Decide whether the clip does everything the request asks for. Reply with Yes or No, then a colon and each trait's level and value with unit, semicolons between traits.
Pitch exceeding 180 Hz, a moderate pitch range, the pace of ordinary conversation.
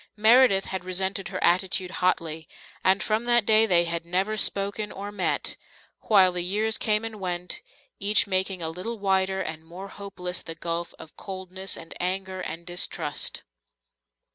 No: high, 190 Hz; narrow, 2.3 semitones; average, 160 wpm